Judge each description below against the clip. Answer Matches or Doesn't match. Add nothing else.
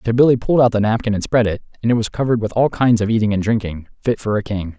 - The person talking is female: Doesn't match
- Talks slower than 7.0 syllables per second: Doesn't match